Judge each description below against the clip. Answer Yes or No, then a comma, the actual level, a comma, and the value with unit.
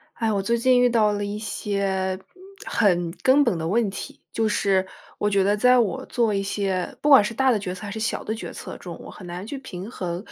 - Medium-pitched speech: No, high, 205 Hz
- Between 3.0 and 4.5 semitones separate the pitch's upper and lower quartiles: Yes, average, 3.4 semitones